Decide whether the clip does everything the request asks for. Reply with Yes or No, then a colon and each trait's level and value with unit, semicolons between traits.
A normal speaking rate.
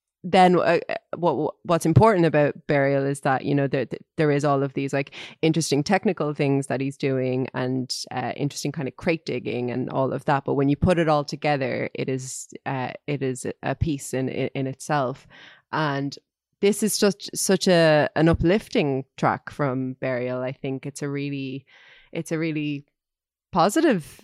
Yes: average, 180 wpm